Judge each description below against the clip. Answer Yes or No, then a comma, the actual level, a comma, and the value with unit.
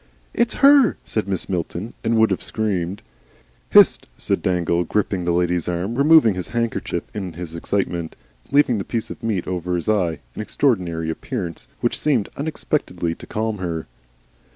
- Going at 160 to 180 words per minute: Yes, average, 165 wpm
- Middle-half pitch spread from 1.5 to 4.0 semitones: No, average, 4.7 semitones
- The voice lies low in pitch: Yes, very low, 95 Hz